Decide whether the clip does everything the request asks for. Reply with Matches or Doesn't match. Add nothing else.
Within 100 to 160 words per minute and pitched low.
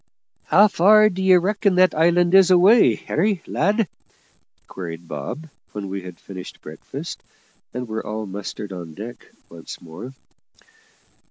Doesn't match